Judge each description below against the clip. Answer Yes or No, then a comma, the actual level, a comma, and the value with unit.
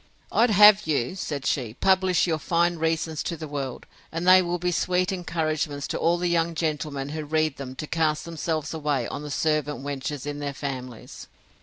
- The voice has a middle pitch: Yes, medium, 155 Hz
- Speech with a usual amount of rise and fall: Yes, average, 3.1 semitones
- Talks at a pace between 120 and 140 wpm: No, average, 190 wpm